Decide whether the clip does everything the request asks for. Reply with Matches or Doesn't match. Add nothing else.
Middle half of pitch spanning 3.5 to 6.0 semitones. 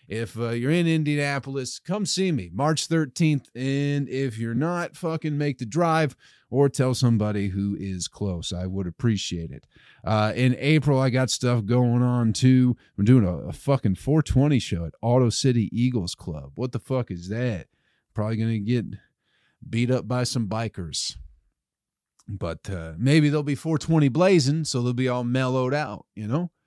Matches